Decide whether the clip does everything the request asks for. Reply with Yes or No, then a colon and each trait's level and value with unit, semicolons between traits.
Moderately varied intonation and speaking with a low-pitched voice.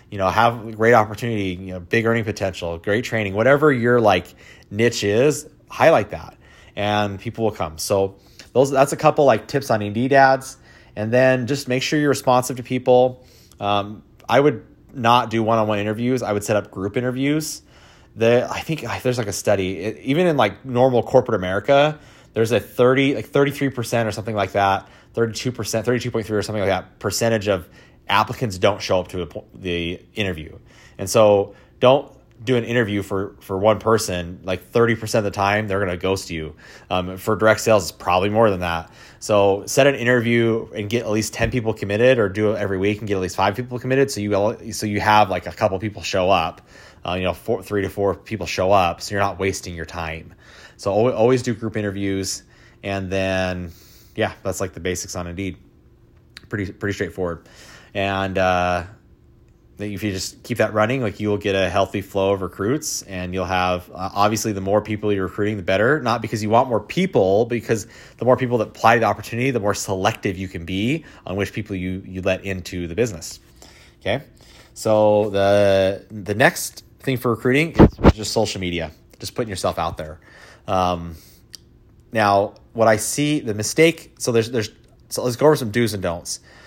Yes: average, 3.7 semitones; low, 105 Hz